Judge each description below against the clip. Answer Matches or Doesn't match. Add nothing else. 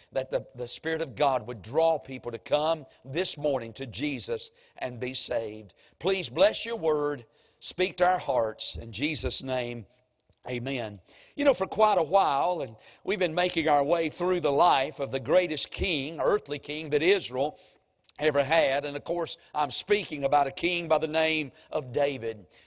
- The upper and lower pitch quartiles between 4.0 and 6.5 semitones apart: Matches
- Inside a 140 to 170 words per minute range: Doesn't match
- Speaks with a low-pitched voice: Doesn't match